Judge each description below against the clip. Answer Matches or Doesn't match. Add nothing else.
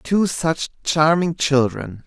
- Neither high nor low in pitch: Matches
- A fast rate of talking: Doesn't match